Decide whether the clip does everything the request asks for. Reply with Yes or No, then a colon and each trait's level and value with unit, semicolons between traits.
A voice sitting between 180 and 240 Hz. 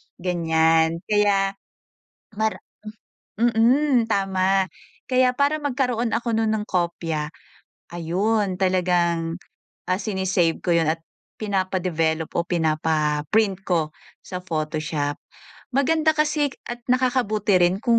Yes: high, 190 Hz